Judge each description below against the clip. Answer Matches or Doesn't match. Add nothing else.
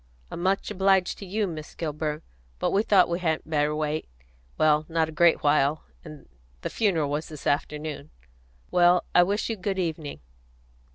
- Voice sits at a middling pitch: Matches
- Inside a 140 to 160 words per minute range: Doesn't match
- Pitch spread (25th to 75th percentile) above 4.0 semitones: Doesn't match